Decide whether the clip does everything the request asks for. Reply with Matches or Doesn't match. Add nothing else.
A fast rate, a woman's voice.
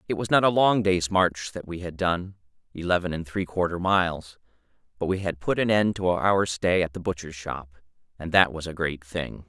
Doesn't match